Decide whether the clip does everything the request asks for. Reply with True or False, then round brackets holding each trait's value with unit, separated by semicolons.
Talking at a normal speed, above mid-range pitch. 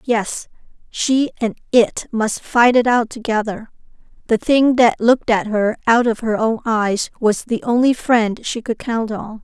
True (180 wpm; 230 Hz)